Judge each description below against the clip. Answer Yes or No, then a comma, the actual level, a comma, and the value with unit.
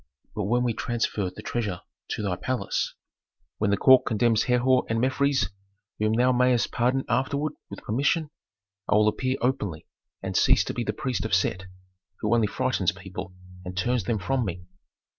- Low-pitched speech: Yes, low, 115 Hz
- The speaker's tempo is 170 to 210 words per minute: Yes, average, 175 wpm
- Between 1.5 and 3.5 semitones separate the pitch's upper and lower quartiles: No, average, 4.2 semitones